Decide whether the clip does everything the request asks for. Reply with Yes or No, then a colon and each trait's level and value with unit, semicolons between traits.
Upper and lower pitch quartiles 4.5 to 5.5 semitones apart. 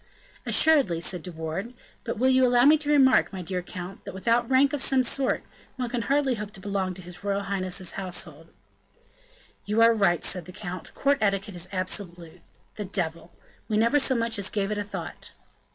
Yes: average, 5.1 semitones